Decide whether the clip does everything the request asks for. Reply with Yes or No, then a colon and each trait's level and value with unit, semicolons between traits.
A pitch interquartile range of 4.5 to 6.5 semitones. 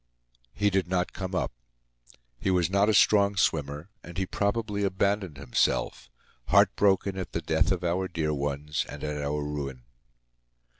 Yes: average, 5.0 semitones